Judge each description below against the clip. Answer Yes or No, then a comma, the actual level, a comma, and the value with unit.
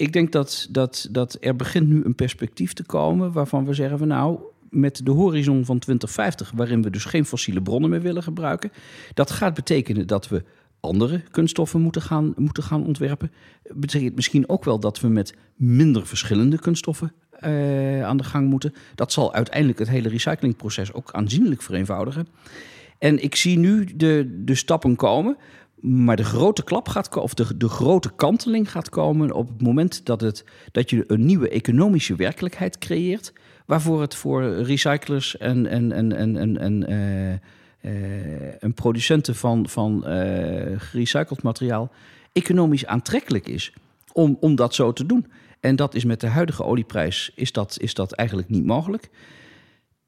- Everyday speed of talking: Yes, average, 170 wpm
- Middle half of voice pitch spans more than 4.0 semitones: Yes, average, 5.3 semitones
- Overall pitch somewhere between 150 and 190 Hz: No, low, 130 Hz